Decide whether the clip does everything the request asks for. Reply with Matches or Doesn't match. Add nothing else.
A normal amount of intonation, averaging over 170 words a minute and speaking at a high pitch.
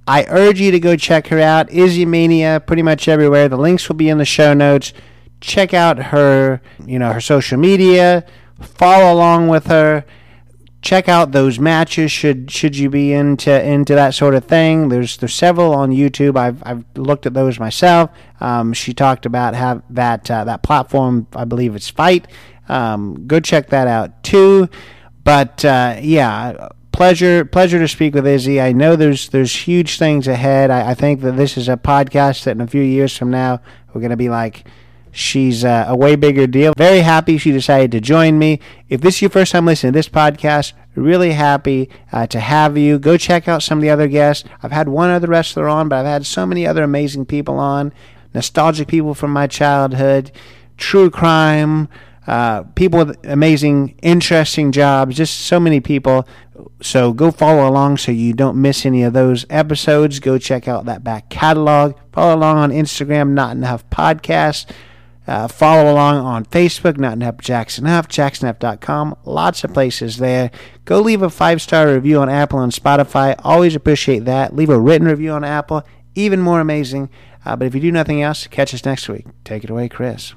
Doesn't match